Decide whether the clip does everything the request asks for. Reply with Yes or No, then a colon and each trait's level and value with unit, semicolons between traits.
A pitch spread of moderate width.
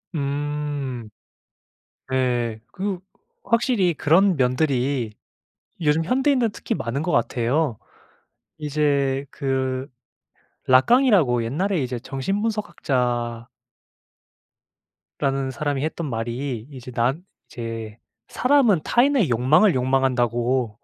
Yes: average, 5.0 semitones